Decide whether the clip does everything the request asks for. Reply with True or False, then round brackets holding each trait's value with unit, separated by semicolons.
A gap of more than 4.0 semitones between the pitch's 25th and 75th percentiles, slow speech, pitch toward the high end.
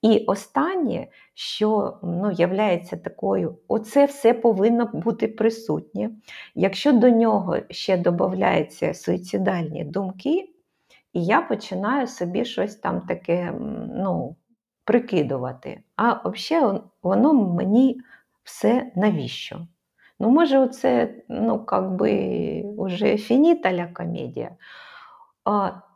True (4.4 semitones; 95 wpm; 220 Hz)